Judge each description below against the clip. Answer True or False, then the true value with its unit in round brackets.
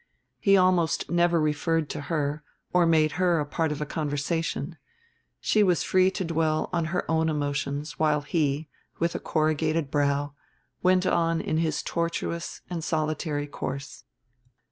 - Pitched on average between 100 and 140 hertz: False (160 Hz)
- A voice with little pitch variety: True (2.3 semitones)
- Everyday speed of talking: True (145 wpm)